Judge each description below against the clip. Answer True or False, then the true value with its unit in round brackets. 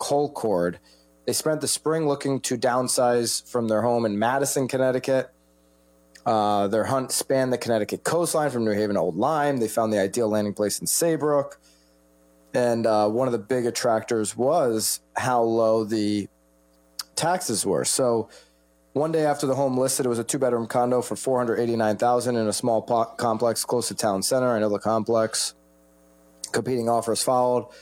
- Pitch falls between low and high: False (115 Hz)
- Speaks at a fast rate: False (175 wpm)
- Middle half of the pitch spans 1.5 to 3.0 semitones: False (3.9 semitones)